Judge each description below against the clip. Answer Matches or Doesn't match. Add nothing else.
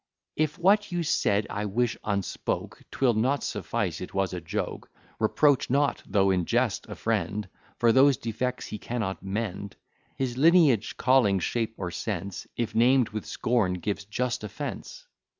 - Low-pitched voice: Matches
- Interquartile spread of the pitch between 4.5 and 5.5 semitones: Matches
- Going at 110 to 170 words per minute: Matches